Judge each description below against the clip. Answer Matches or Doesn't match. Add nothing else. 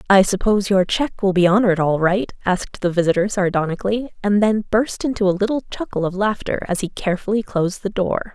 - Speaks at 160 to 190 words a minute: Doesn't match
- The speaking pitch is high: Matches